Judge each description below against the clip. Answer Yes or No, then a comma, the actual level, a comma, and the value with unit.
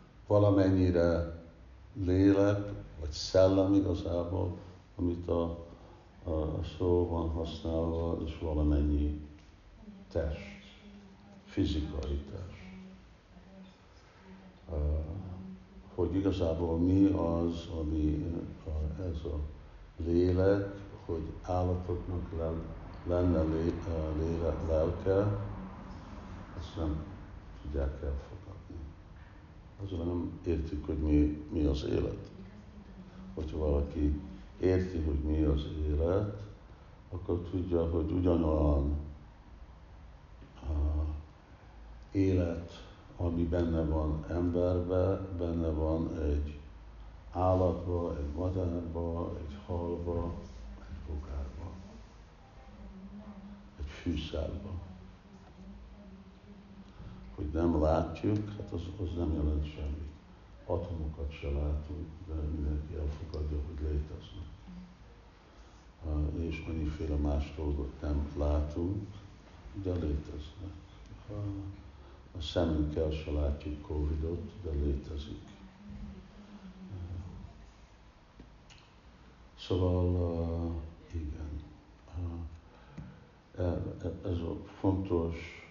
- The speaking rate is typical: No, slow, 75 wpm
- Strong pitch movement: No, average, 3.5 semitones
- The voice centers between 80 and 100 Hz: Yes, very low, 85 Hz